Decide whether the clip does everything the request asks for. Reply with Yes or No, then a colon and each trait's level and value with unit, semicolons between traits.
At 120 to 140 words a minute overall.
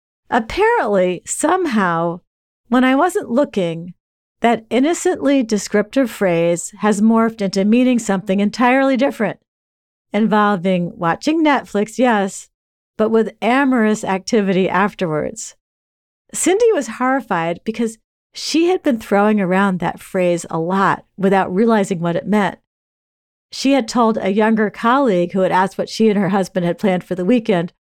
Yes: slow, 135 wpm